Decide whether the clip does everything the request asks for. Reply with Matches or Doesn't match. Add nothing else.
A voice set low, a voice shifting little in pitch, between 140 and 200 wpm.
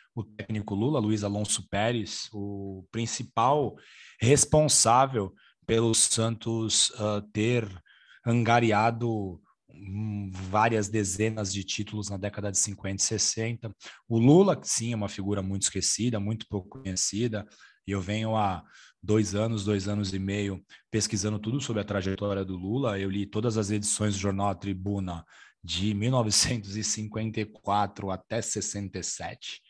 Doesn't match